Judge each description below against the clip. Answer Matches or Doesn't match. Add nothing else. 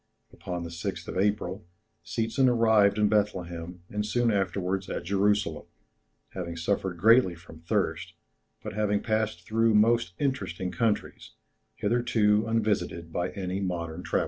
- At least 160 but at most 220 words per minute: Doesn't match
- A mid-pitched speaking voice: Doesn't match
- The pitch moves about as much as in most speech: Matches